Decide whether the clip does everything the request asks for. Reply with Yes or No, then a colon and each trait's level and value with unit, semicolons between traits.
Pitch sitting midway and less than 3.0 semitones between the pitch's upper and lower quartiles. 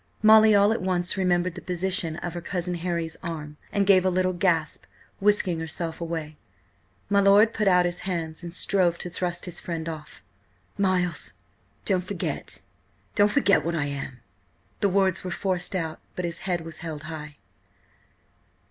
Yes: medium, 175 Hz; narrow, 2.5 semitones